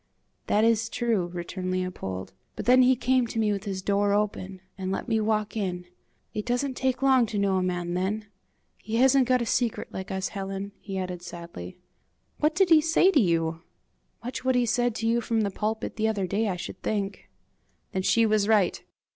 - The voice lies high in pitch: Yes, high, 210 Hz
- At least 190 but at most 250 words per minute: Yes, fast, 205 wpm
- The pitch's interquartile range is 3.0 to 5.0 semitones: Yes, average, 4.1 semitones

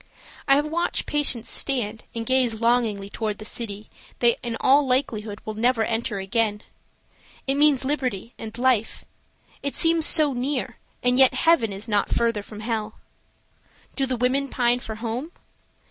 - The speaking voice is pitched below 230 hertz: No, high, 240 Hz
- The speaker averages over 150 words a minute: Yes, average, 160 wpm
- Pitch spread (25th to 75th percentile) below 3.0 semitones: No, average, 3.6 semitones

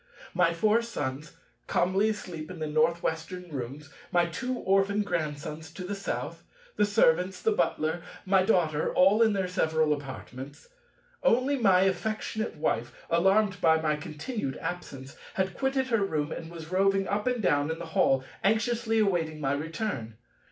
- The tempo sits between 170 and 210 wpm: No, average, 160 wpm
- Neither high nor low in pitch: Yes, medium, 180 Hz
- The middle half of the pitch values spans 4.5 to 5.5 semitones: Yes, average, 4.9 semitones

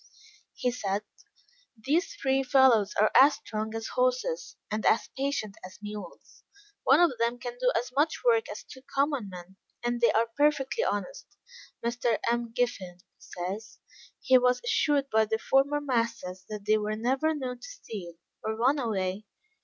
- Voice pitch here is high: Yes, high, 240 Hz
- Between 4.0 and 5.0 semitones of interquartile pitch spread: Yes, average, 4.4 semitones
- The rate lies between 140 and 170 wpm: Yes, average, 160 wpm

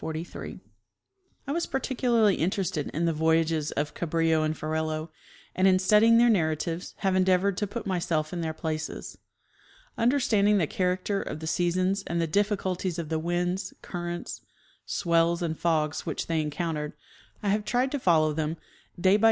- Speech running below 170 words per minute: Yes, average, 160 wpm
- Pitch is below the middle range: No, medium, 175 Hz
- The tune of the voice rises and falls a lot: No, average, 3.8 semitones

